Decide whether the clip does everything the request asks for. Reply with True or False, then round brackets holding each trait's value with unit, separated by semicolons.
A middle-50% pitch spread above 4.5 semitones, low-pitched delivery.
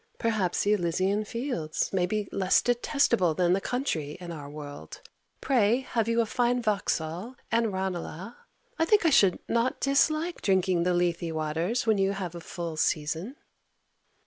False (5.4 semitones; 195 Hz)